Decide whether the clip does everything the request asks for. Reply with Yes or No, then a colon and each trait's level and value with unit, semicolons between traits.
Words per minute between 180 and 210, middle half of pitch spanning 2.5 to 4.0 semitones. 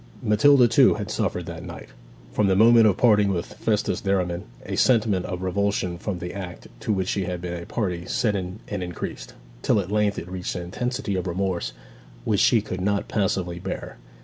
Yes: average, 200 wpm; average, 2.9 semitones